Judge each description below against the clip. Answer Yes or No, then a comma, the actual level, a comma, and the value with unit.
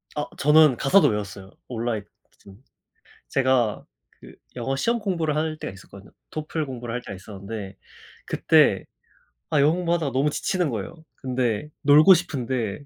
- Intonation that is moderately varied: No, wide, 5.8 semitones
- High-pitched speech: No, low, 130 Hz